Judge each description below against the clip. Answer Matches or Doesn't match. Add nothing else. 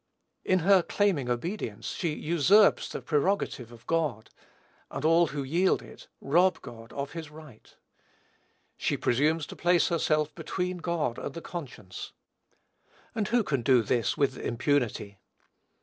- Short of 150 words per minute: Matches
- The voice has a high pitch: Doesn't match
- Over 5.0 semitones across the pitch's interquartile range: Matches